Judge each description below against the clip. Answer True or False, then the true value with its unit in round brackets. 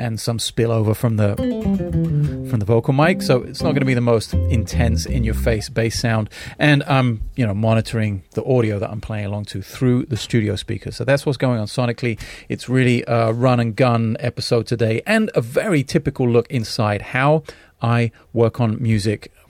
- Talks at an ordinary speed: True (190 wpm)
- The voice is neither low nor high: False (115 Hz)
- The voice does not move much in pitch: False (3.0 semitones)